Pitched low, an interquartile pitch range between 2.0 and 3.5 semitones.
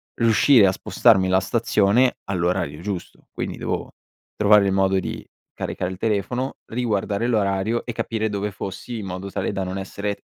Yes: low, 100 Hz; average, 2.7 semitones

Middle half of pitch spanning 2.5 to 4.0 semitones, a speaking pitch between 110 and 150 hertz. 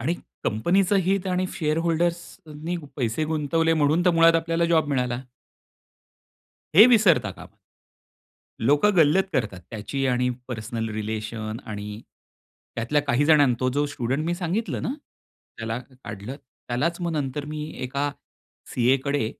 No: wide, 5.6 semitones; medium, 145 Hz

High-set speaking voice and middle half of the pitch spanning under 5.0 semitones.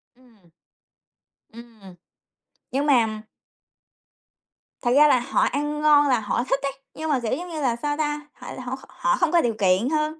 Yes: very high, 270 Hz; average, 4.2 semitones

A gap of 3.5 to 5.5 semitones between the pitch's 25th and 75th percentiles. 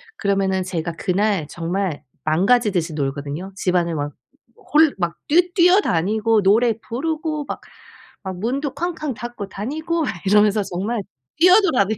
No: wide, 7.8 semitones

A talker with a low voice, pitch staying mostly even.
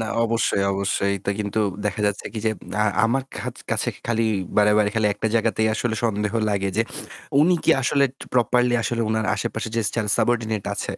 Yes: low, 110 Hz; narrow, 2.0 semitones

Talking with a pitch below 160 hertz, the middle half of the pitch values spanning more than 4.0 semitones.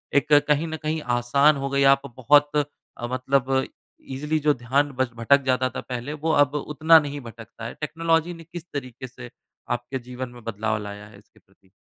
No: low, 135 Hz; average, 3.5 semitones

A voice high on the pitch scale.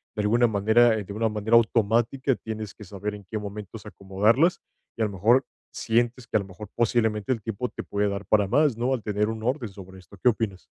No: low, 110 Hz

